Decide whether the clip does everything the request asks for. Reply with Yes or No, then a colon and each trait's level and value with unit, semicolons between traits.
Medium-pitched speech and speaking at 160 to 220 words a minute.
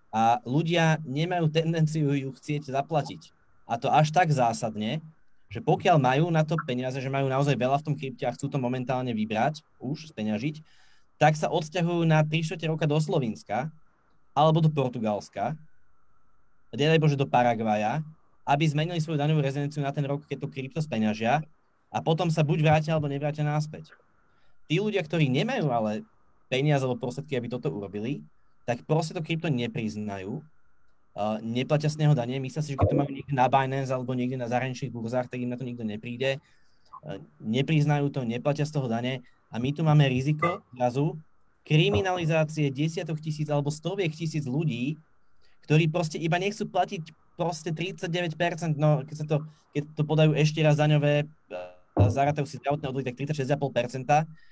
Yes: medium, 145 Hz; fast, 165 wpm